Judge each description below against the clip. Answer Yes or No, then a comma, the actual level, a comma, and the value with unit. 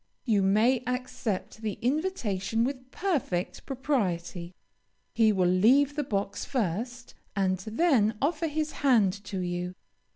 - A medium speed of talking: No, slow, 125 wpm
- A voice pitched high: Yes, high, 225 Hz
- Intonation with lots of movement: Yes, wide, 5.9 semitones